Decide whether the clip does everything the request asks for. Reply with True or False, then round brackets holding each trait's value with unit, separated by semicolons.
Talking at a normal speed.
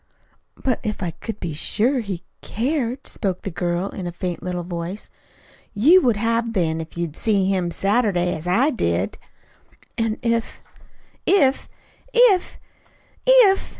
True (150 wpm)